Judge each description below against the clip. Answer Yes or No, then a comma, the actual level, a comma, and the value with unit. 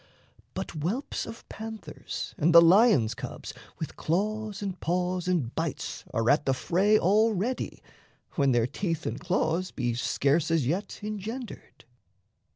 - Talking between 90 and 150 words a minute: Yes, average, 140 wpm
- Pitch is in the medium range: Yes, medium, 180 Hz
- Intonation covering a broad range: Yes, wide, 6.1 semitones